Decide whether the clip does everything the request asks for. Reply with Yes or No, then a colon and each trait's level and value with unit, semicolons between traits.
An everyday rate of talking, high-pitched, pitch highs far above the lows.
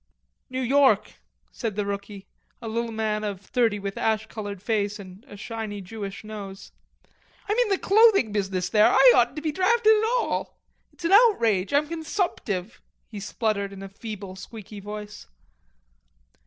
No: average, 165 wpm; high, 215 Hz; average, 5.0 semitones